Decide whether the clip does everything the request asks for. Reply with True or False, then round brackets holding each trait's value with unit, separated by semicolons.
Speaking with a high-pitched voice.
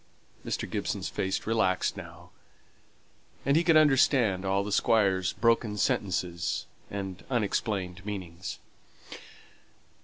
False (100 Hz)